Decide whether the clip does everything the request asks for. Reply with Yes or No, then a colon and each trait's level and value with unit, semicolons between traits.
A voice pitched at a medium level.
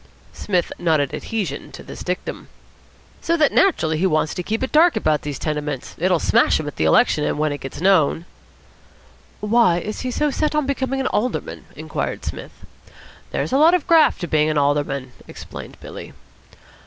Yes: medium, 175 Hz